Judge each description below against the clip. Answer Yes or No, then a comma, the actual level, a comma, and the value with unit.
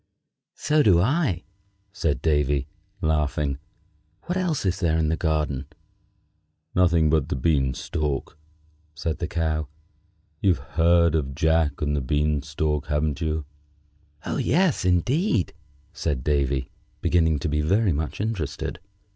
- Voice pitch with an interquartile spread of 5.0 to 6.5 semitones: No, average, 3.1 semitones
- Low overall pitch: Yes, very low, 80 Hz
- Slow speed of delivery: Yes, slow, 130 wpm